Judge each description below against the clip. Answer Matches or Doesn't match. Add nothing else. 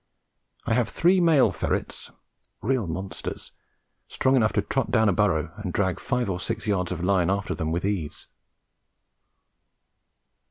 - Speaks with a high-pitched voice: Doesn't match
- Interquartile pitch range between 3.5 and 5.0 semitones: Matches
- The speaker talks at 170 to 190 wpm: Doesn't match